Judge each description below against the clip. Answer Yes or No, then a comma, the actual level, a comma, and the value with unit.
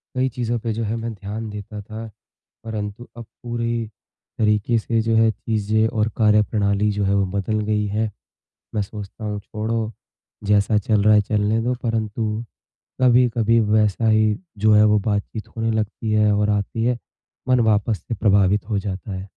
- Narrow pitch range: Yes, narrow, 1.5 semitones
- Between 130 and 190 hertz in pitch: No, low, 110 Hz